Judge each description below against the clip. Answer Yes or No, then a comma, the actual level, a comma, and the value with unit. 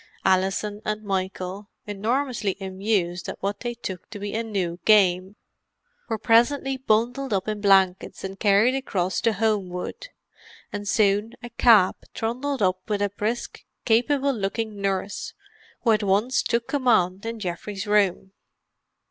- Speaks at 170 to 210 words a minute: No, average, 140 wpm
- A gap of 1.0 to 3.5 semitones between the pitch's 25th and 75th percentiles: Yes, average, 3.1 semitones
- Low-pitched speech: No, high, 210 Hz